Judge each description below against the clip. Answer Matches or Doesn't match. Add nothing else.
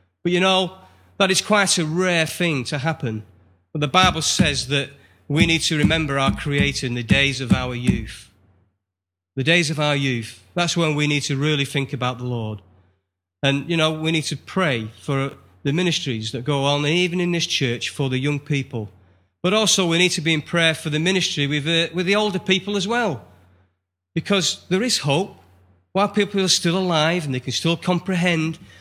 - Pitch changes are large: Matches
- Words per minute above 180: Matches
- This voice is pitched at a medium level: Matches